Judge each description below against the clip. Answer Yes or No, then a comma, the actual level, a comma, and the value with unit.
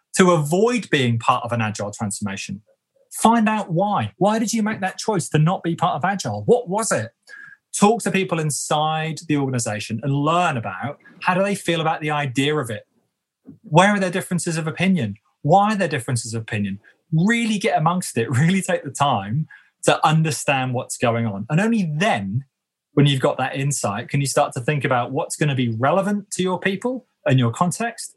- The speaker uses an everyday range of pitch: No, wide, 7.0 semitones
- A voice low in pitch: No, medium, 155 Hz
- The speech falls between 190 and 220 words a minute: Yes, average, 200 wpm